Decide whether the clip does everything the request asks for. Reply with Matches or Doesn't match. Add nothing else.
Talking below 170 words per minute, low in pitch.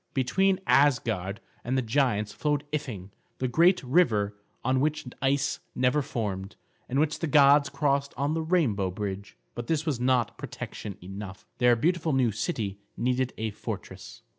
Matches